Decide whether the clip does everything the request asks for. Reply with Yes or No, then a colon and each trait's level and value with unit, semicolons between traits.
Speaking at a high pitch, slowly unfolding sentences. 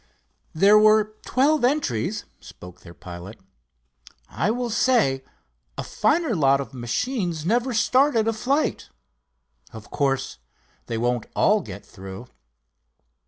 Yes: high, 200 Hz; slow, 120 wpm